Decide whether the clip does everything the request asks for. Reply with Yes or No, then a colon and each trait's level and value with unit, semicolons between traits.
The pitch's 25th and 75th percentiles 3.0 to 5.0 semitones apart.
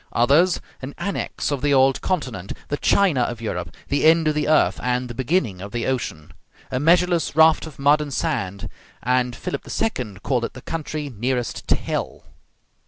Yes: average, 4.5 semitones